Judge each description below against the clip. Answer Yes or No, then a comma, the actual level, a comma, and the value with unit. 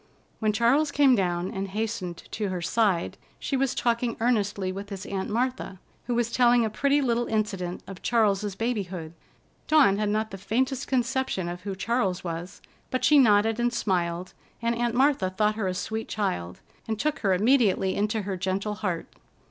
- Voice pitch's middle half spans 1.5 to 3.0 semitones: No, average, 4.0 semitones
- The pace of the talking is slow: No, average, 180 wpm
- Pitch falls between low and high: No, high, 215 Hz